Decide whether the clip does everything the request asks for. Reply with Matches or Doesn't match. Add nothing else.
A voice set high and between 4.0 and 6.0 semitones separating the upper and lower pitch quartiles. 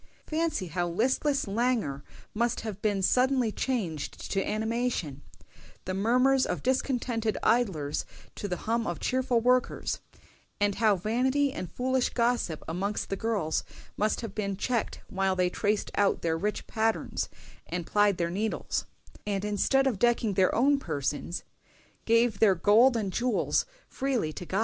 Matches